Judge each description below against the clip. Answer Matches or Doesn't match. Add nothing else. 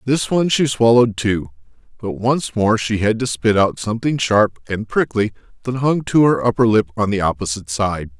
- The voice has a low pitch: Matches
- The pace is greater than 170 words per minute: Matches